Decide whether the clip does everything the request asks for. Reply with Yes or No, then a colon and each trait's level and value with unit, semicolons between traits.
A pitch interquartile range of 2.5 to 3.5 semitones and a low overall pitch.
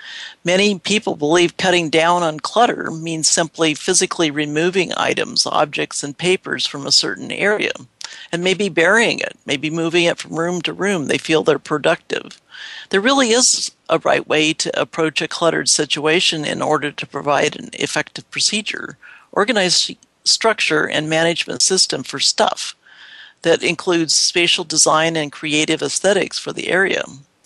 No: average, 2.8 semitones; medium, 165 Hz